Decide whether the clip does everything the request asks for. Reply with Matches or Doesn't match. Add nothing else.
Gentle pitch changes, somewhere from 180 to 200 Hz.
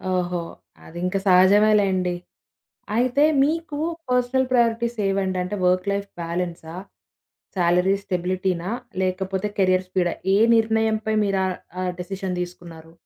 Doesn't match